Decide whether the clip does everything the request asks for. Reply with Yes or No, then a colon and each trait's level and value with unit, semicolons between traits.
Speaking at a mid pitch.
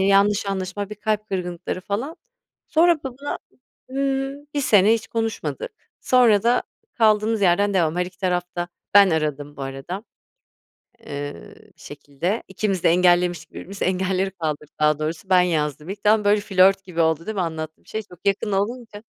No: high, 195 Hz